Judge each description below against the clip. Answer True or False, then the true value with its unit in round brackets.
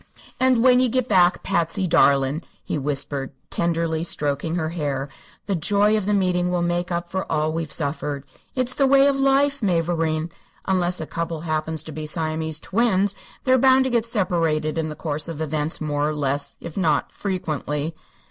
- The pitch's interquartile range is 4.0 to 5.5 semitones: True (4.5 semitones)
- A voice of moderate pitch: True (165 Hz)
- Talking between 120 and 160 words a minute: False (185 wpm)